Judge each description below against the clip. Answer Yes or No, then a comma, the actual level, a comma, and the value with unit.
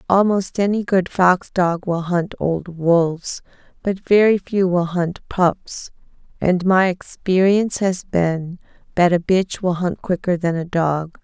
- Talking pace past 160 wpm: No, average, 155 wpm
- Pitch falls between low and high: Yes, medium, 180 Hz